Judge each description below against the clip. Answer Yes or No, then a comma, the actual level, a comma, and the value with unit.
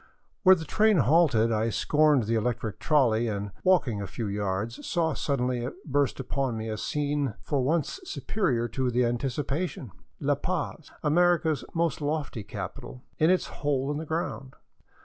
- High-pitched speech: No, low, 135 Hz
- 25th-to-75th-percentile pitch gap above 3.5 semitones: Yes, average, 5.2 semitones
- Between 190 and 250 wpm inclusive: No, average, 160 wpm